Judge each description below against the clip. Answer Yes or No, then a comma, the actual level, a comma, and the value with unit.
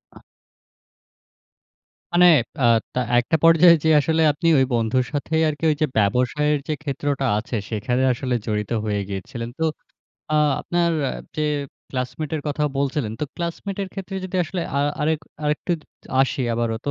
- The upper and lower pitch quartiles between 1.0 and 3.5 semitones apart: No, average, 4.6 semitones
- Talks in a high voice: No, medium, 145 Hz